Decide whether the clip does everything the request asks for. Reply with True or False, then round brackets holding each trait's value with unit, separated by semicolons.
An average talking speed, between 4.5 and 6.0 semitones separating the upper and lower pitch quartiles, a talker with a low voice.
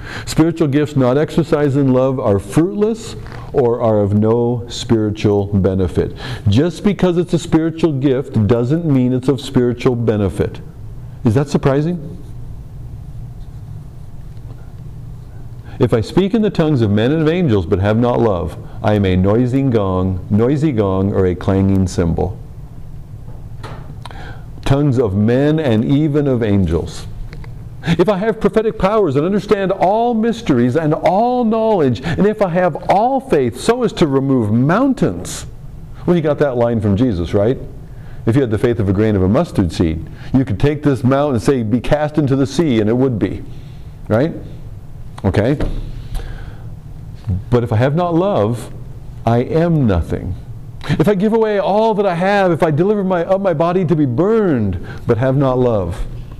True (165 wpm; 5.2 semitones; 130 Hz)